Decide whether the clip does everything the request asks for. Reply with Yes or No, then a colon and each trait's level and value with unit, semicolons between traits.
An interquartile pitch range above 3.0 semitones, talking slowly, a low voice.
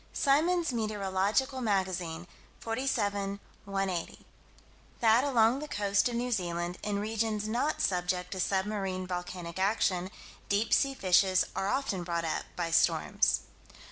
No: average, 3.8 semitones; slow, 125 wpm; high, 200 Hz